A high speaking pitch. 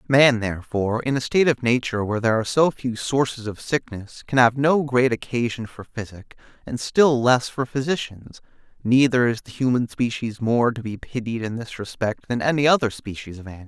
No: low, 120 Hz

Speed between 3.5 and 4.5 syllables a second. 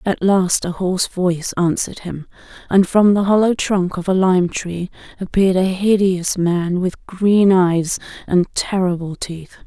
Yes: 4.2 syllables/s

